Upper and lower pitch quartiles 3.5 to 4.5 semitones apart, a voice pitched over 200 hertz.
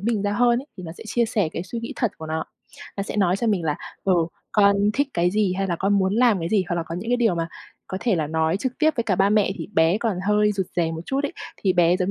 No: average, 4.2 semitones; high, 195 Hz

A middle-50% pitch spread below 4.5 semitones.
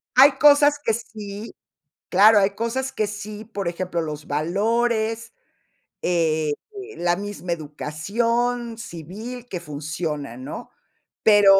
No: wide, 5.6 semitones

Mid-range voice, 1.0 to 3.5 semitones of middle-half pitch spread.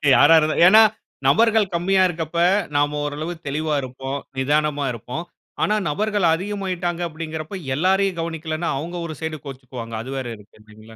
No: medium, 155 Hz; average, 4.2 semitones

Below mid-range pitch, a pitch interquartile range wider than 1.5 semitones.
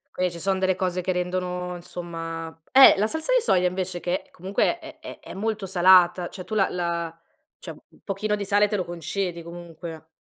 No: medium, 180 Hz; narrow, 2.2 semitones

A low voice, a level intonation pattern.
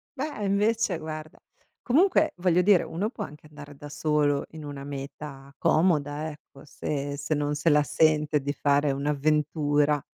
No: medium, 150 Hz; narrow, 2.2 semitones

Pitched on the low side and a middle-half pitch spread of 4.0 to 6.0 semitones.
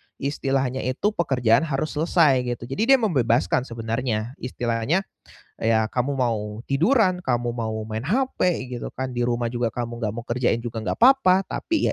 Yes: low, 125 Hz; average, 5.0 semitones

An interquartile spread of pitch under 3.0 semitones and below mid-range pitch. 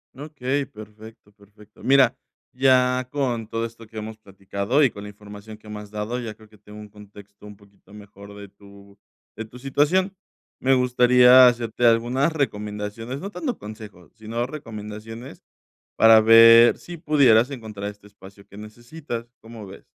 No: average, 3.3 semitones; low, 110 Hz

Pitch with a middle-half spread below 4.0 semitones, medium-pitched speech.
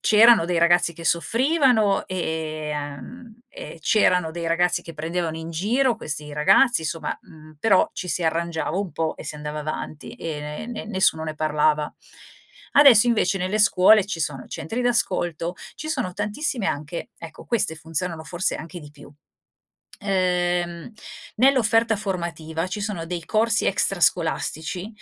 No: average, 4.9 semitones; medium, 175 Hz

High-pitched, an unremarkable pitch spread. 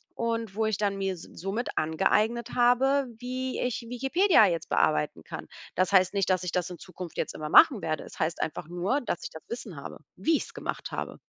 No: high, 195 Hz; wide, 5.7 semitones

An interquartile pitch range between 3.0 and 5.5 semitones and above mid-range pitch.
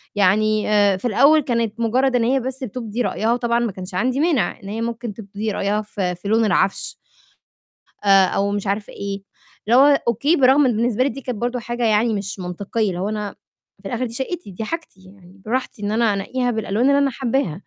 Yes: average, 3.7 semitones; high, 220 Hz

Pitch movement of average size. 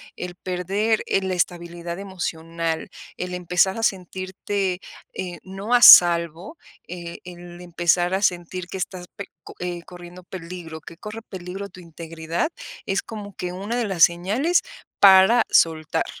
No: narrow, 2.0 semitones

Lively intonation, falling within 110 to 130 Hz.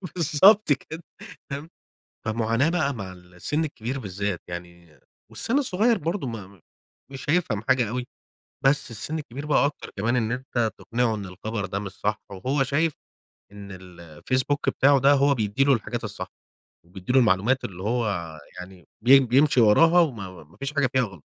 Yes: wide, 6.2 semitones; low, 120 Hz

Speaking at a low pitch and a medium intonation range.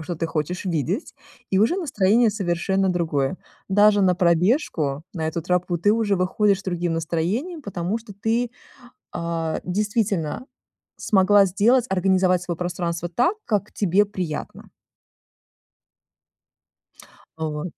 No: medium, 185 Hz; average, 3.4 semitones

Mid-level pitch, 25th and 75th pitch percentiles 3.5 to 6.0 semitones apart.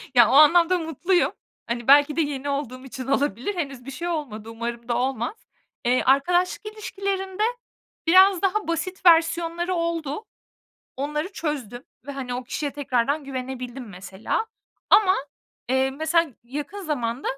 No: very high, 285 Hz; average, 5.2 semitones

